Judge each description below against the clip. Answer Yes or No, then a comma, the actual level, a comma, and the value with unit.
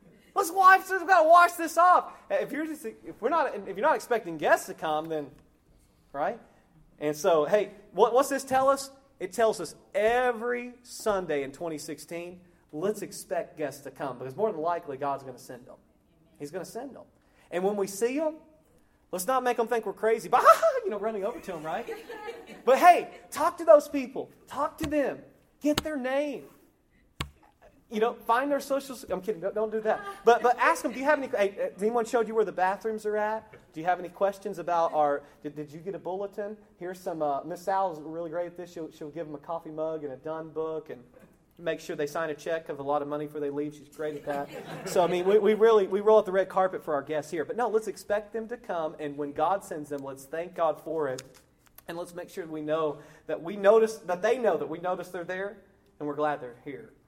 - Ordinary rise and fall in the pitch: No, wide, 7.2 semitones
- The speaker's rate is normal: No, fast, 240 wpm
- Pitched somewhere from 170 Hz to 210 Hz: Yes, high, 190 Hz